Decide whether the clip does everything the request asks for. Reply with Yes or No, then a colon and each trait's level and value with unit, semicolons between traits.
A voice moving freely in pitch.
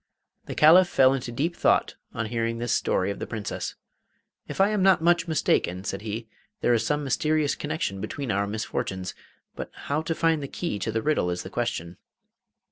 Yes: wide, 7.0 semitones